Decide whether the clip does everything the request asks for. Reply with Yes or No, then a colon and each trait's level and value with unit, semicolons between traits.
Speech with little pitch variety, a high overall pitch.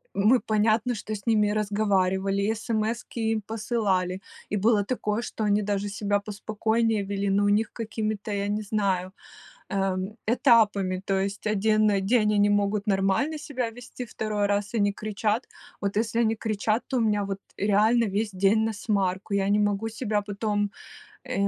Yes: narrow, 1.8 semitones; high, 210 Hz